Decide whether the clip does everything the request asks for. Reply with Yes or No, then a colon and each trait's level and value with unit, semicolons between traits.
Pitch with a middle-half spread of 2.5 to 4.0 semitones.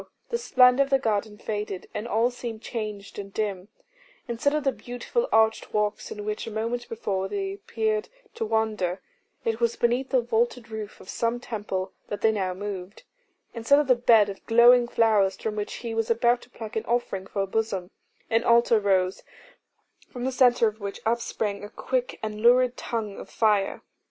Yes: average, 2.8 semitones